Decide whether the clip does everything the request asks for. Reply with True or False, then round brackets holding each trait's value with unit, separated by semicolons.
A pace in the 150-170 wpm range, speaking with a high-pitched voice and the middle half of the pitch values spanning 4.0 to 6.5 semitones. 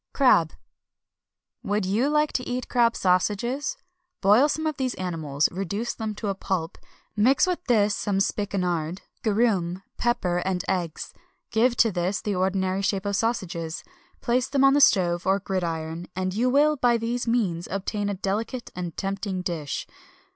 True (160 wpm; 200 Hz; 4.7 semitones)